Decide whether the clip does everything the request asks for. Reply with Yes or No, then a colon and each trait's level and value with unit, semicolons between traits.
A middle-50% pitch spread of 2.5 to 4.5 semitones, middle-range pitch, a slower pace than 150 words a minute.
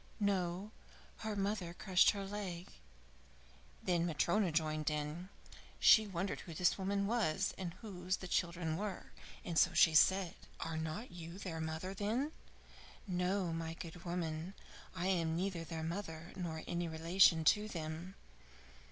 Yes: average, 3.0 semitones; medium, 175 Hz; average, 140 wpm